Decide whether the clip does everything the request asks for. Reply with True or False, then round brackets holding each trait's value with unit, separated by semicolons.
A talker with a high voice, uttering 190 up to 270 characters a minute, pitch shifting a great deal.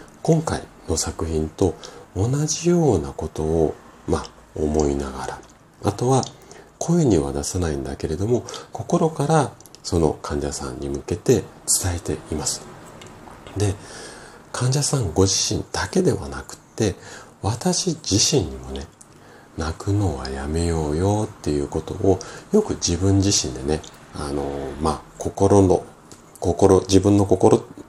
False (95 Hz; 235 characters per minute; 7.2 semitones)